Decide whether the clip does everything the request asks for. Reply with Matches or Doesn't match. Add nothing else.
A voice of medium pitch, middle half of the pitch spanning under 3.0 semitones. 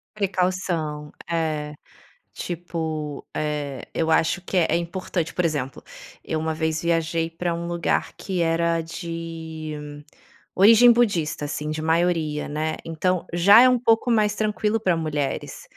Matches